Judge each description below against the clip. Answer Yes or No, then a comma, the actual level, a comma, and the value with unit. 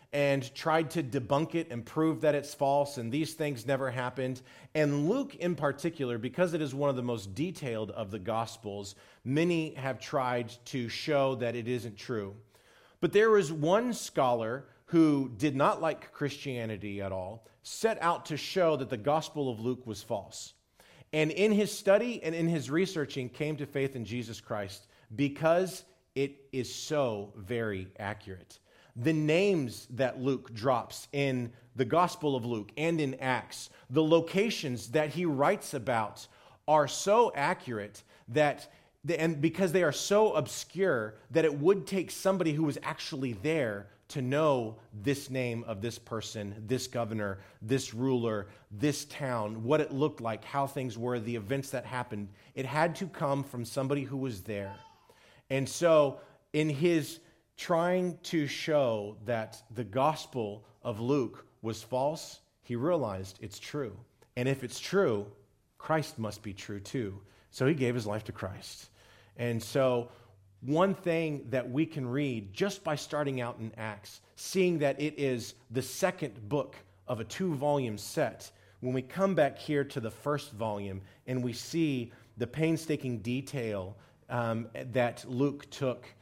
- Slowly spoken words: No, average, 160 wpm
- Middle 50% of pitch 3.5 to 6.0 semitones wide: Yes, average, 5.2 semitones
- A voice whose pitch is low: Yes, low, 130 Hz